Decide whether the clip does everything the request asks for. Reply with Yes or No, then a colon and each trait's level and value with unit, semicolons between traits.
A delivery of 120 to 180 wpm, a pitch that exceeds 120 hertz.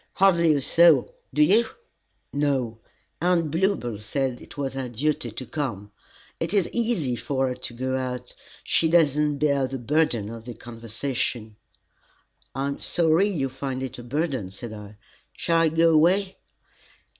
Yes: average, 160 wpm; medium, 140 Hz